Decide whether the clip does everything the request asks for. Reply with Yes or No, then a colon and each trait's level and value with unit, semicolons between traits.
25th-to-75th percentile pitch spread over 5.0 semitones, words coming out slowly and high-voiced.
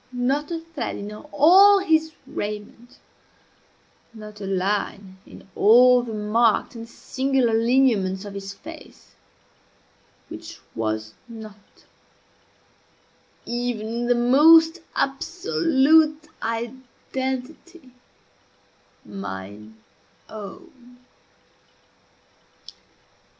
Yes: wide, 5.6 semitones; slow, 80 wpm; high, 240 Hz